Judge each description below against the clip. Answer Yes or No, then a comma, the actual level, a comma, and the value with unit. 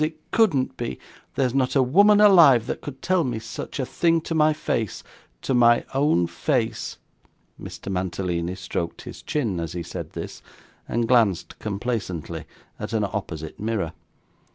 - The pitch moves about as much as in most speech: No, wide, 7.9 semitones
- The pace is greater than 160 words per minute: No, average, 155 wpm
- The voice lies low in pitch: Yes, low, 120 Hz